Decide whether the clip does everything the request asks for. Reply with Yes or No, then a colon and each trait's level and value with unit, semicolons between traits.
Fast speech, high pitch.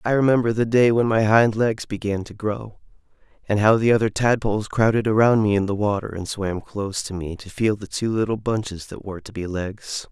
No: fast, 225 wpm; low, 105 Hz